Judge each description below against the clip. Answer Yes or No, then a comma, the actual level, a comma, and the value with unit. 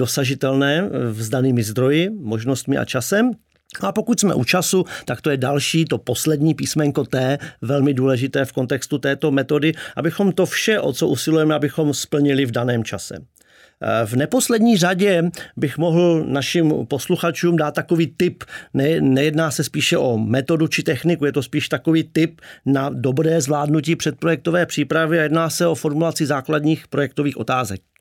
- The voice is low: No, medium, 155 Hz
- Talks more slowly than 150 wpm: No, average, 155 wpm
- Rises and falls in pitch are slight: No, average, 3.5 semitones